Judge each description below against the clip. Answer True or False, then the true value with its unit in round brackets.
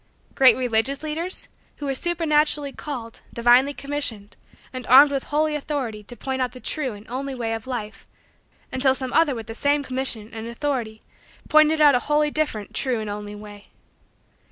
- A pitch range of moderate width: True (4.4 semitones)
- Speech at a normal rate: True (180 wpm)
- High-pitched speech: True (260 Hz)